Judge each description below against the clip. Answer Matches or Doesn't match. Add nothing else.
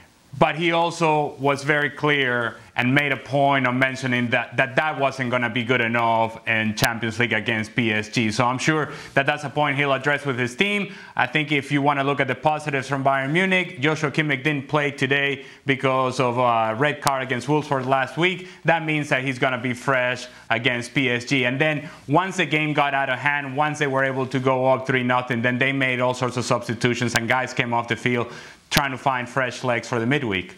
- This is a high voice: Doesn't match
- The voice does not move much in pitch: Doesn't match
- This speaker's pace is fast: Matches